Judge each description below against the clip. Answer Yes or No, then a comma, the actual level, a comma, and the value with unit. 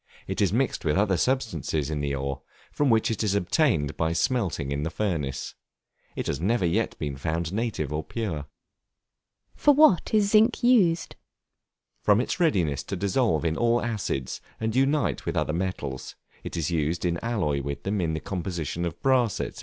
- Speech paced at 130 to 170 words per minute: No, average, 180 wpm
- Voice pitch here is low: Yes, very low, 90 Hz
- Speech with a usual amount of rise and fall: No, wide, 7.5 semitones